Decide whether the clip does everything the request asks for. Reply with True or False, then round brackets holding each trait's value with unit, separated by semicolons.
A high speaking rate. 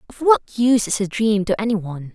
True (250 wpm)